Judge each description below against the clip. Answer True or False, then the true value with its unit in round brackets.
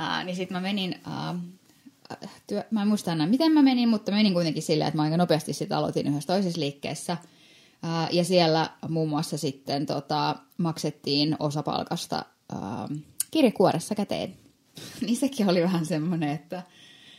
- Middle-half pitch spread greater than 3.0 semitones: True (4.0 semitones)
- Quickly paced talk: True (160 wpm)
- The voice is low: False (175 Hz)